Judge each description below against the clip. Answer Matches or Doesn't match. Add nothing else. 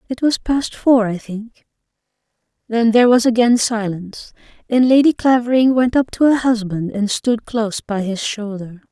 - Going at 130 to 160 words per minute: Doesn't match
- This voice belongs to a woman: Matches